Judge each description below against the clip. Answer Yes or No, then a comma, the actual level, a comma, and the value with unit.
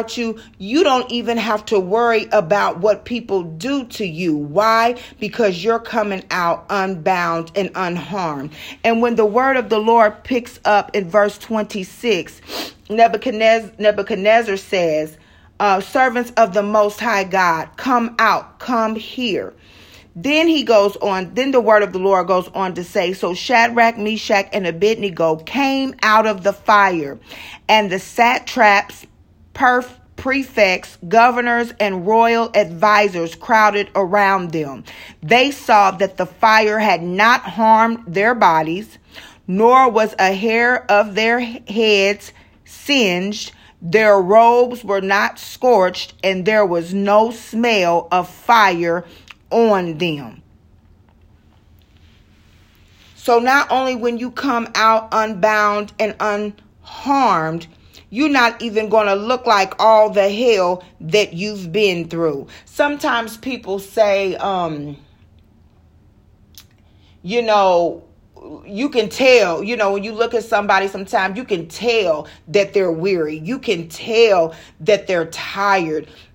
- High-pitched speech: Yes, high, 210 Hz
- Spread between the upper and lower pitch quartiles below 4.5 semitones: Yes, average, 3.9 semitones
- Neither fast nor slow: No, slow, 130 wpm